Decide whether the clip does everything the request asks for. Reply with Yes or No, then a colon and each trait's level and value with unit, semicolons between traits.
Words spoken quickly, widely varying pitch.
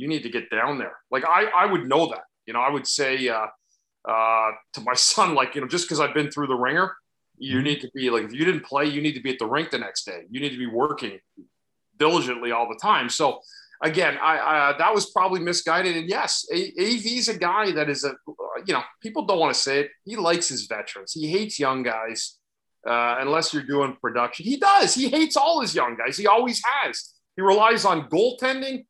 Yes: fast, 235 wpm; wide, 8.5 semitones